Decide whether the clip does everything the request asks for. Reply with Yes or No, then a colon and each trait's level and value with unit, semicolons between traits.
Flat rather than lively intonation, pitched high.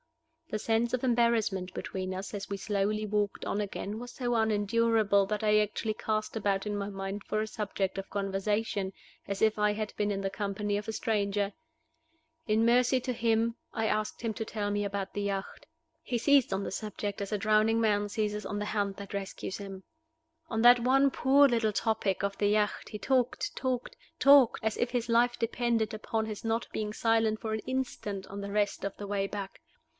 Yes: narrow, 2.2 semitones; high, 215 Hz